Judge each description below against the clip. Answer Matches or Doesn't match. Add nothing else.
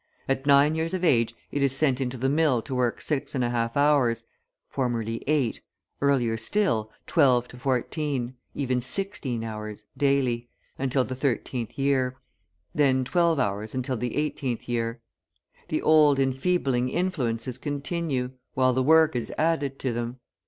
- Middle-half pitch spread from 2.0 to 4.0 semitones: Matches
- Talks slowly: Doesn't match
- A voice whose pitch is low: Matches